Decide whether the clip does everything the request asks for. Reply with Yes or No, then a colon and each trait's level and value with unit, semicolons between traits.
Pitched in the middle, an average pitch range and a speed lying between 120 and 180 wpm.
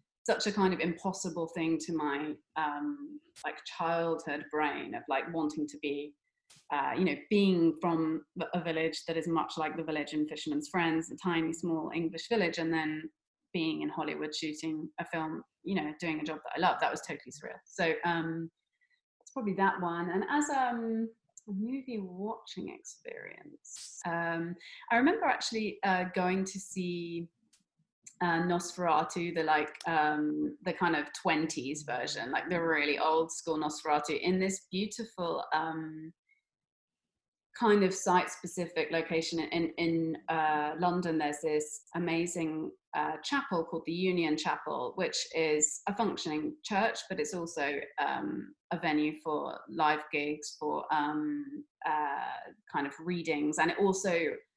Yes: medium, 165 Hz; average, 3.5 semitones; average, 150 wpm